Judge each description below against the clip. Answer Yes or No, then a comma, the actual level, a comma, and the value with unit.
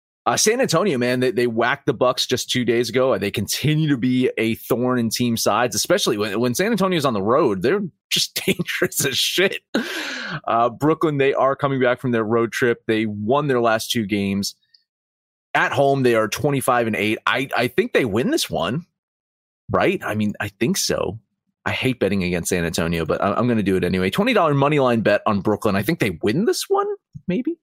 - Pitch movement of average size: Yes, average, 4.6 semitones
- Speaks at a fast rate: Yes, fast, 215 wpm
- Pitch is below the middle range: Yes, low, 120 Hz